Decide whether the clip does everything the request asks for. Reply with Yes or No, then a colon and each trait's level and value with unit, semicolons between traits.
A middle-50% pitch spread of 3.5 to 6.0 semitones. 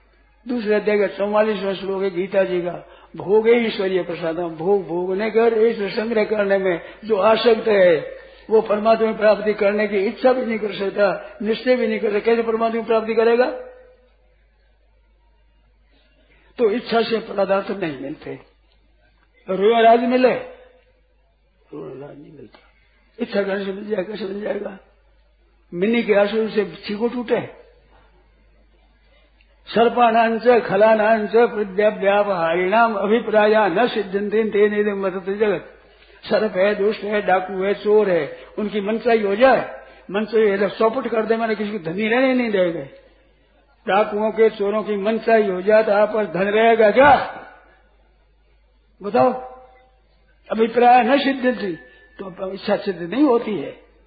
No: narrow, 2.5 semitones